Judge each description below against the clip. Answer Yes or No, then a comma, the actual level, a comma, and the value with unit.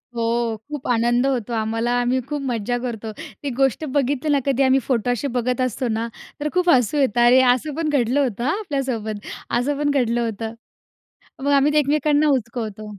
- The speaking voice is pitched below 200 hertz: No, very high, 250 Hz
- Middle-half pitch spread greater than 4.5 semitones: No, average, 3.6 semitones